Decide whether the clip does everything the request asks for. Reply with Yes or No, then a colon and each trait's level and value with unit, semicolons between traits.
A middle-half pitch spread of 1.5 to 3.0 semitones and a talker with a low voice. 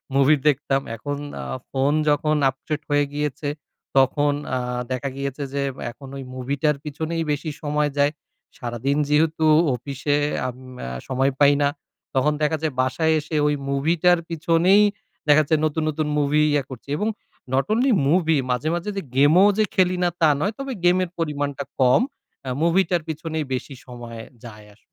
No: average, 2.7 semitones; medium, 145 Hz